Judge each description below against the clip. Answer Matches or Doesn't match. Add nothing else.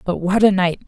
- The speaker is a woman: Matches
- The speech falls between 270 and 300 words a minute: Matches